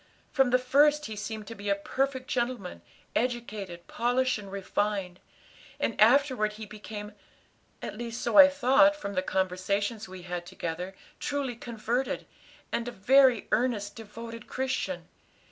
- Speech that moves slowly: No, average, 145 wpm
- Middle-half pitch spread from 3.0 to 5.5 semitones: Yes, average, 4.2 semitones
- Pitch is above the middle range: Yes, high, 225 Hz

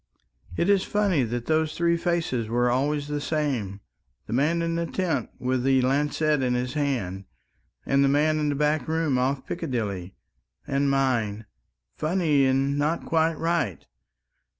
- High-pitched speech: No, medium, 140 Hz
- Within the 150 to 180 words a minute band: Yes, average, 155 wpm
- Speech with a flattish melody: No, average, 4.1 semitones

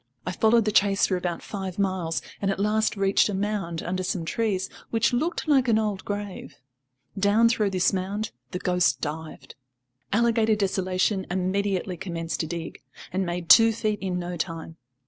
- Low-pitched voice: No, high, 195 Hz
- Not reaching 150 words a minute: No, average, 170 wpm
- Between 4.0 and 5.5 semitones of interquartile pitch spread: No, average, 3.0 semitones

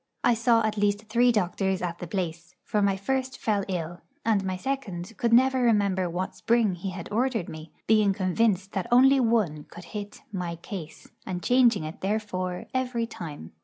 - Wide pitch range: No, average, 4.4 semitones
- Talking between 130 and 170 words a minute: No, average, 180 wpm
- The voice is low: No, high, 200 Hz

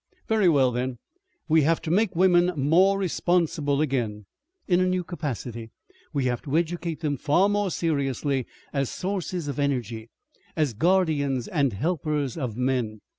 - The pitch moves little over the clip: No, average, 5.2 semitones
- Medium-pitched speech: Yes, medium, 150 Hz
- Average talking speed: Yes, average, 150 wpm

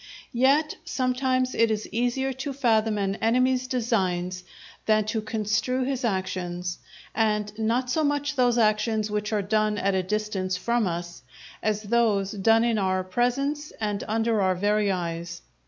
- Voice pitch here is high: Yes, high, 215 Hz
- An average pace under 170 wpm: Yes, average, 155 wpm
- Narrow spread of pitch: No, average, 3.9 semitones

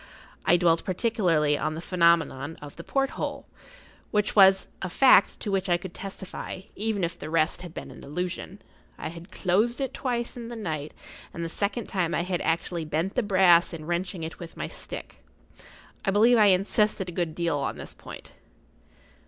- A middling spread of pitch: Yes, average, 3.5 semitones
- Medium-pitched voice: Yes, medium, 180 Hz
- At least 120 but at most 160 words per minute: No, average, 185 wpm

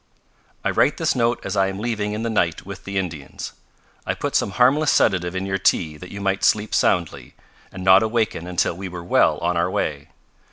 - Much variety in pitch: No, average, 3.3 semitones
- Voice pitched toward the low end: Yes, very low, 95 Hz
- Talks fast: Yes, fast, 210 wpm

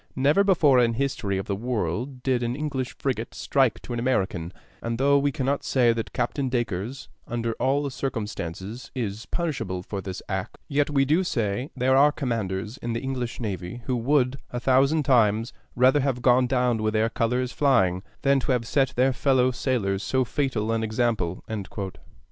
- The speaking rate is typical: Yes, average, 175 wpm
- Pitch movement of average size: Yes, average, 3.3 semitones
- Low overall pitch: Yes, low, 125 Hz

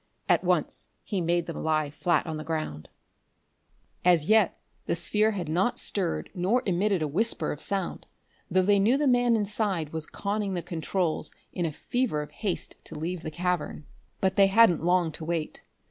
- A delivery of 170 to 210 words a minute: Yes, average, 180 wpm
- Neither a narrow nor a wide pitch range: Yes, average, 4.1 semitones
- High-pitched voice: No, medium, 180 Hz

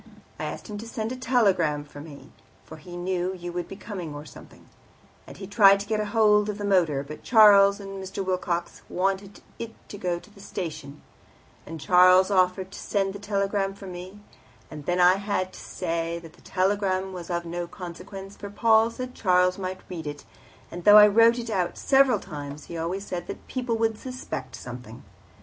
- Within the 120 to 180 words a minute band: No, average, 195 wpm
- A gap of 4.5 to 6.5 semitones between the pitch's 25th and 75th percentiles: No, average, 2.9 semitones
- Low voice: No, high, 190 Hz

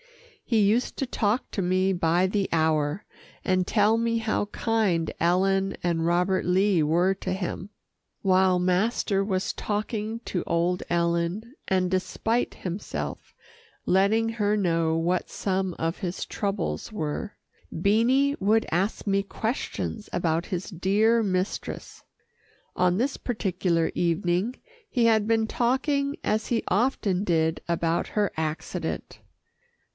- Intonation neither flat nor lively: Yes, average, 3.8 semitones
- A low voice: No, high, 190 Hz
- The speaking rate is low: Yes, slow, 130 wpm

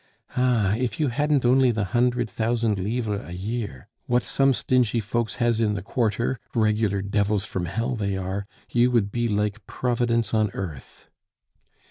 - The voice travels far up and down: No, average, 3.1 semitones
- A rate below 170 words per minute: Yes, average, 160 wpm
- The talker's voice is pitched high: No, low, 115 Hz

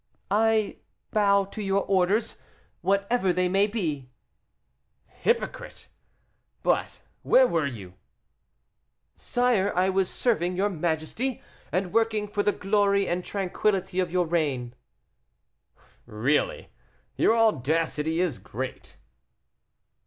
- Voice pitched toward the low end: No, high, 190 Hz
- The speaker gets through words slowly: Yes, slow, 105 wpm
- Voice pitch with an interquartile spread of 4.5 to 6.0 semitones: No, average, 4.1 semitones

